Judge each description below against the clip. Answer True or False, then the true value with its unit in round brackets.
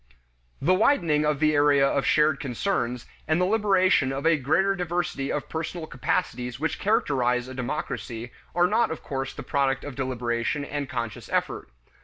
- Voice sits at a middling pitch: True (145 Hz)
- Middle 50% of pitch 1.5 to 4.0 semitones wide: False (4.5 semitones)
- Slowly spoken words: False (165 wpm)